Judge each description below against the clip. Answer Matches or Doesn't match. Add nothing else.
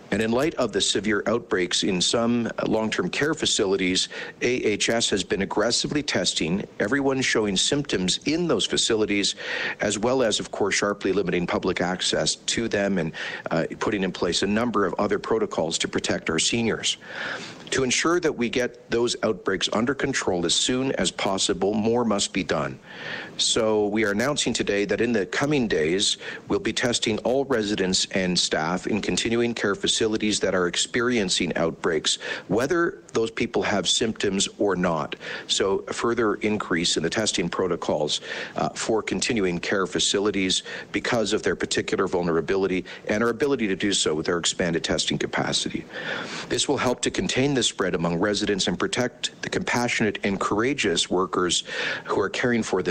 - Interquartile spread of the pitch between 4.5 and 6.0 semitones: Doesn't match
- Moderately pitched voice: Doesn't match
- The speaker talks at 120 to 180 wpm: Matches